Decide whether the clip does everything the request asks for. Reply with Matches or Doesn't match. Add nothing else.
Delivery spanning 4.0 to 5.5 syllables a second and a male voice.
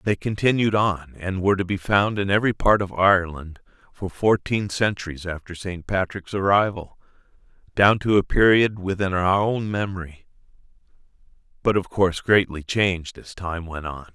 Matches